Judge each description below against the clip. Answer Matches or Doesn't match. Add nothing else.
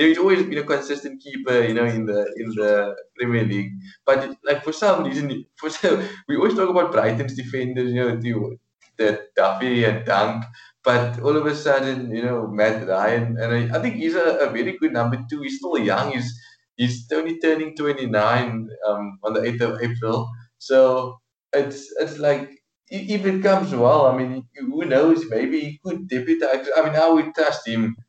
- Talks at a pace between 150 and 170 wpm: Doesn't match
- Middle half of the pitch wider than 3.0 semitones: Matches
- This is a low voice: Matches